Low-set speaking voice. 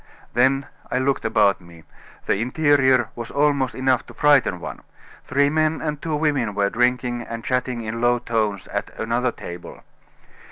Yes: low, 125 Hz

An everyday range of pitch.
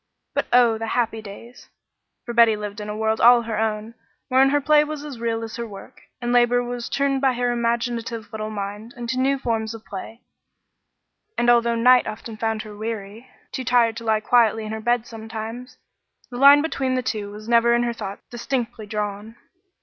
No: narrow, 2.0 semitones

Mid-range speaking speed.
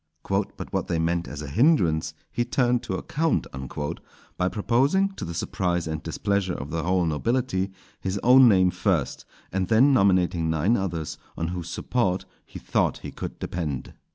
Yes: average, 165 wpm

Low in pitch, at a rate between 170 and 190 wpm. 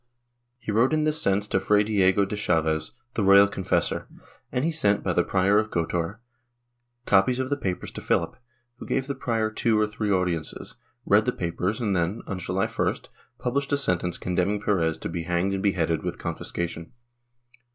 Yes: low, 100 Hz; average, 185 wpm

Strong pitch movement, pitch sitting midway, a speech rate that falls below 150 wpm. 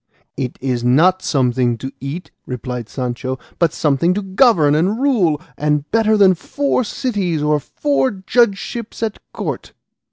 Yes: wide, 7.4 semitones; medium, 160 Hz; average, 140 wpm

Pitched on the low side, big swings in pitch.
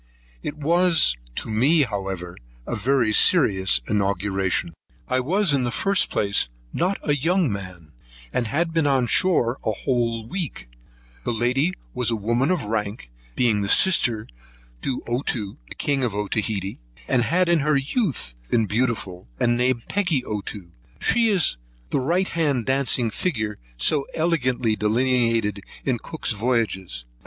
Yes: low, 120 Hz; wide, 6.0 semitones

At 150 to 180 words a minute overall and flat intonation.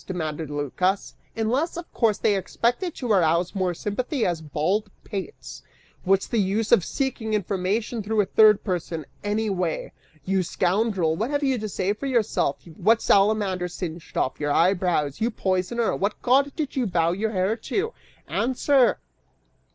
No: average, 155 wpm; average, 4.3 semitones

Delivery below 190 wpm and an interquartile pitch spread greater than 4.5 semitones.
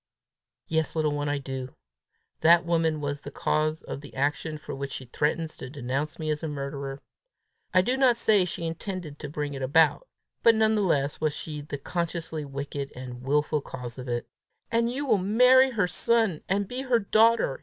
No: average, 195 wpm; wide, 5.6 semitones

